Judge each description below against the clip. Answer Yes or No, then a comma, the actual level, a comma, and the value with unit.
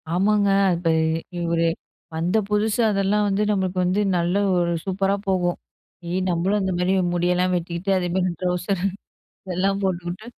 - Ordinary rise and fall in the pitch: No, narrow, 2.0 semitones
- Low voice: No, medium, 185 Hz